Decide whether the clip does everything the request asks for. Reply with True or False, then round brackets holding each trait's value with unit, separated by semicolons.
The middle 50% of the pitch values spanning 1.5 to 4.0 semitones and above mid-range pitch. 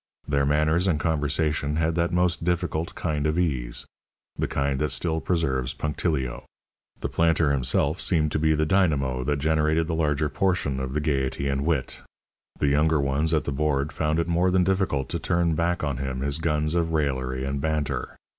False (2.9 semitones; 75 Hz)